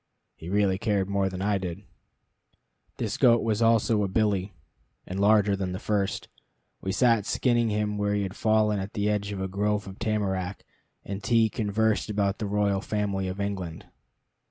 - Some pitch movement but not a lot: No, narrow, 1.7 semitones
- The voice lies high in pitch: No, low, 100 Hz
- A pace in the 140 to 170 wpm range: No, average, 180 wpm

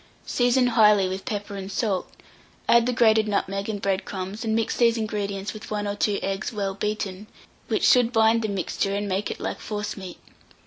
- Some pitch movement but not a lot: No, narrow, 2.1 semitones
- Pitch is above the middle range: Yes, high, 210 Hz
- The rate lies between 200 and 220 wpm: No, average, 190 wpm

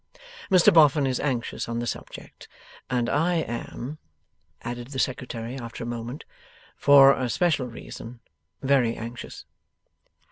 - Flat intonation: No, average, 3.2 semitones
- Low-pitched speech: Yes, low, 125 Hz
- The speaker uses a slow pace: Yes, slow, 130 wpm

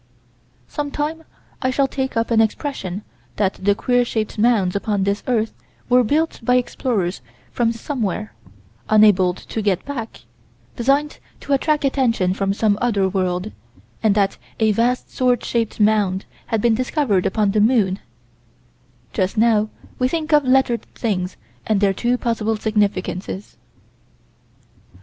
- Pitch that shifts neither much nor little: Yes, average, 4.0 semitones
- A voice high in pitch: Yes, high, 220 Hz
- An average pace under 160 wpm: Yes, average, 140 wpm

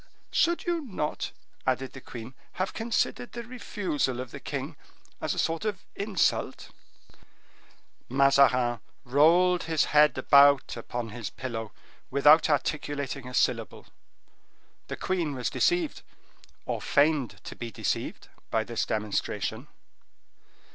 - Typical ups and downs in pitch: No, wide, 6.3 semitones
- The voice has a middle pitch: Yes, medium, 145 Hz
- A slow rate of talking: Yes, slow, 120 wpm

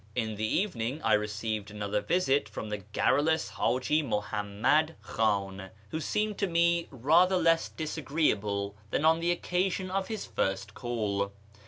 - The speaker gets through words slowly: No, average, 150 wpm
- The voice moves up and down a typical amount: No, wide, 7.9 semitones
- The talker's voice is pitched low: Yes, low, 130 Hz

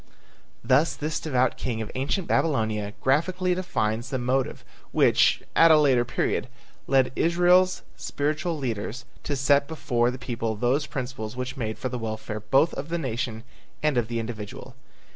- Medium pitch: No, low, 130 Hz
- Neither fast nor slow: Yes, average, 160 wpm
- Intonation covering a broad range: No, average, 4.6 semitones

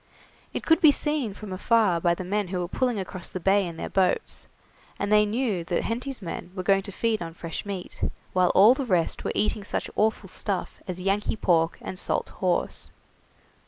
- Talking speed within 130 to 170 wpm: No, average, 200 wpm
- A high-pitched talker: Yes, high, 195 Hz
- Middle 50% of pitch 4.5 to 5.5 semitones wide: No, average, 3.2 semitones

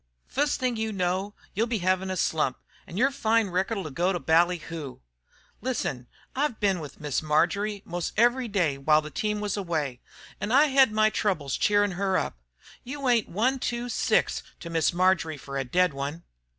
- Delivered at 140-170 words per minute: No, average, 185 wpm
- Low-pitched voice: No, high, 190 Hz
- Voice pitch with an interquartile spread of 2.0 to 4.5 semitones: No, wide, 5.5 semitones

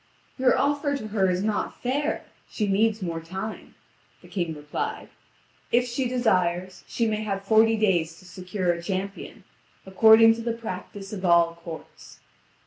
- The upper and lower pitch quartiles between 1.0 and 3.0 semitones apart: No, average, 3.8 semitones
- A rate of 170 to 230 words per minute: No, average, 155 wpm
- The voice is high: Yes, high, 200 Hz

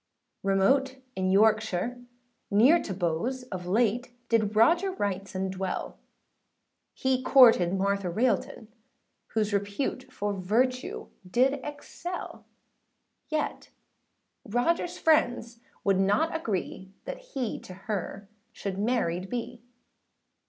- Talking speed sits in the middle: No, slow, 105 wpm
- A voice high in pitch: Yes, high, 220 Hz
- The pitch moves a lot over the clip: No, average, 4.9 semitones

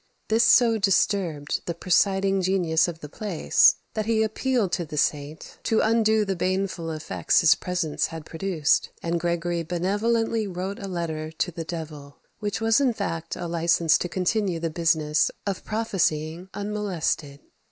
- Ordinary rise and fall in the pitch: Yes, average, 4.2 semitones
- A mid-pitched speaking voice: Yes, medium, 180 Hz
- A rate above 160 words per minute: No, average, 155 wpm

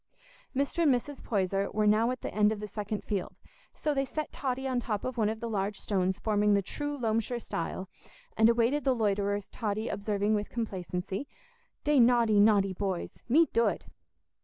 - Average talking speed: Yes, average, 185 wpm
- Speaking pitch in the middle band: No, high, 215 Hz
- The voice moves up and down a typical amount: Yes, average, 3.3 semitones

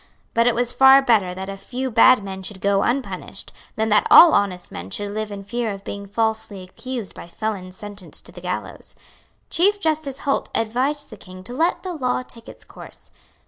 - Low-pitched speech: No, high, 220 Hz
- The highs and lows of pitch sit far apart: No, average, 4.6 semitones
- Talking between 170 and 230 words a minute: Yes, average, 200 wpm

